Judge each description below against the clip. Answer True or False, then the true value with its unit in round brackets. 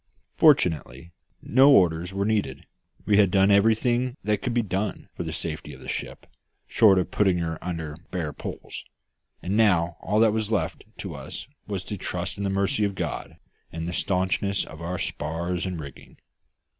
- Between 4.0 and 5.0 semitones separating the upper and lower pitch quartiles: False (3.6 semitones)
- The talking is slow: False (180 wpm)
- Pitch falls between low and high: False (95 Hz)